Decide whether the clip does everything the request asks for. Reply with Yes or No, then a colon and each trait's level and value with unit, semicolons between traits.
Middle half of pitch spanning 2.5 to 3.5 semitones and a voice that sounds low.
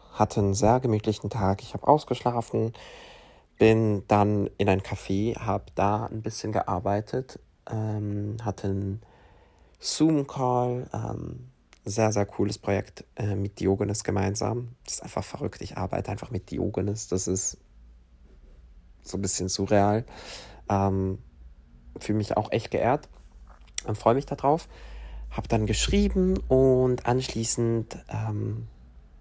Yes: average, 3.2 semitones; low, 105 Hz